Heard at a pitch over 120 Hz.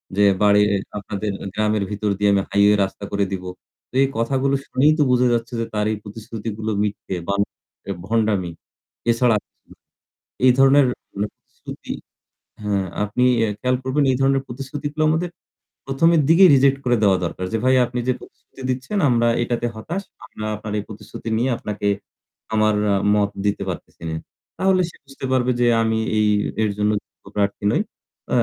No: low, 115 Hz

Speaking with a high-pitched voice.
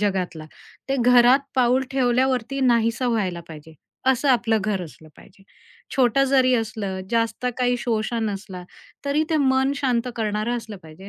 Yes: high, 235 Hz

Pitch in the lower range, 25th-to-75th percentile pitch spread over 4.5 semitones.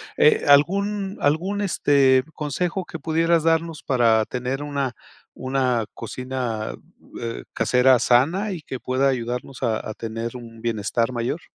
Yes: low, 130 Hz; average, 5.1 semitones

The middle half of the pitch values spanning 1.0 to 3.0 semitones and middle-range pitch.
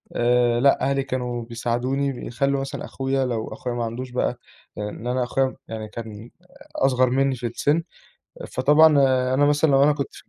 No: narrow, 2.4 semitones; low, 130 Hz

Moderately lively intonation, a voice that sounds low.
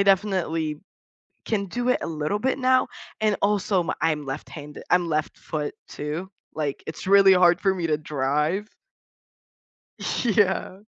No: average, 4.6 semitones; medium, 180 Hz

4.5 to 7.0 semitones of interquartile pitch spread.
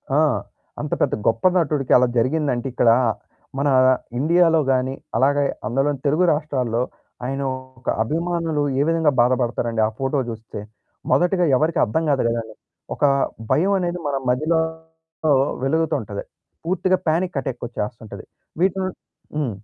Yes: average, 4.8 semitones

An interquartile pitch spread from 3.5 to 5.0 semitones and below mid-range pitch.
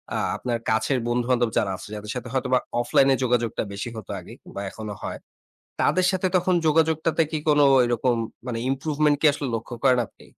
Yes: average, 4.1 semitones; low, 125 Hz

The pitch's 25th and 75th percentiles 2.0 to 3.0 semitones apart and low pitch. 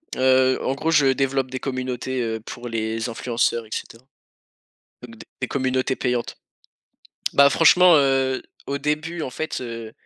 Yes: narrow, 2.6 semitones; low, 130 Hz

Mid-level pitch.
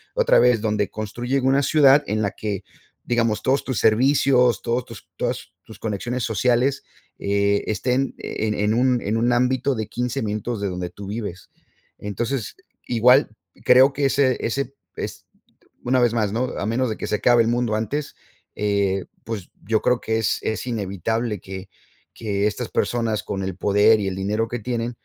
No: low, 115 Hz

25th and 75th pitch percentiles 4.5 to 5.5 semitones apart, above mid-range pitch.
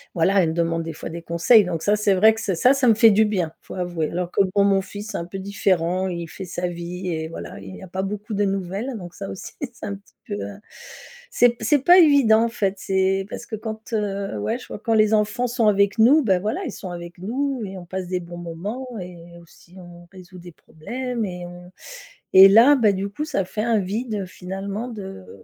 No: average, 3.7 semitones; high, 195 Hz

